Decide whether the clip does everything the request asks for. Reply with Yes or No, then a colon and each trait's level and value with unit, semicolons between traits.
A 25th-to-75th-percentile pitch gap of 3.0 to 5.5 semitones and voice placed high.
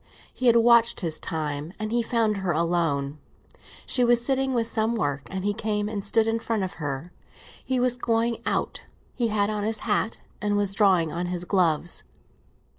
Yes: average, 4.8 semitones; high, 210 Hz